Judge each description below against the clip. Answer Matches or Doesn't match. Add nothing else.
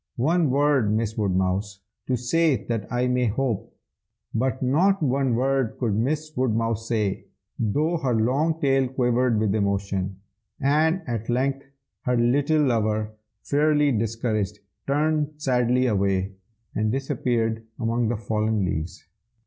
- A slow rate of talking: Matches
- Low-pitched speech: Matches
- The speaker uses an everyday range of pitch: Matches